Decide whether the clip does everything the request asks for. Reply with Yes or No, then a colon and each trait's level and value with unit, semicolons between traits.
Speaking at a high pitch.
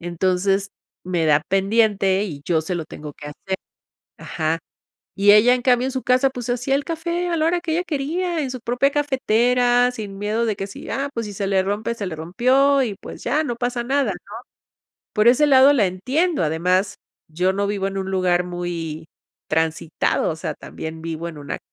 Yes: high, 210 Hz